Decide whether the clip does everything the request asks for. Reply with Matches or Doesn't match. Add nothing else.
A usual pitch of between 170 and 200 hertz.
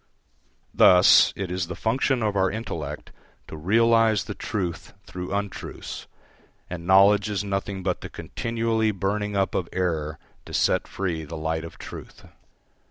Doesn't match